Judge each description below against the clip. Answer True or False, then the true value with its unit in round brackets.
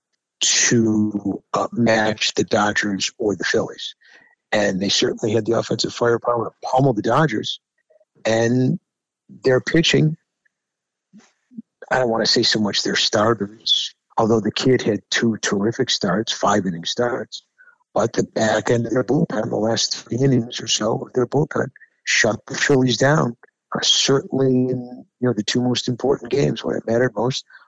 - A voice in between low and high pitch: False (125 Hz)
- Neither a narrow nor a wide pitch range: True (3.2 semitones)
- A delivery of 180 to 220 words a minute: False (155 wpm)